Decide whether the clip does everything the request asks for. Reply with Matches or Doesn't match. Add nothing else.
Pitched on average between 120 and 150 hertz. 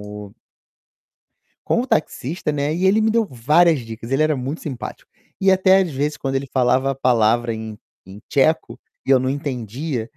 Matches